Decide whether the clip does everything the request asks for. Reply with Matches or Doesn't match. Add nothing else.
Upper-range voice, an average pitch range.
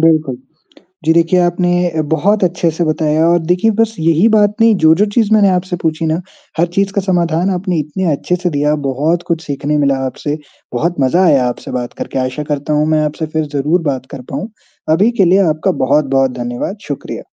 Doesn't match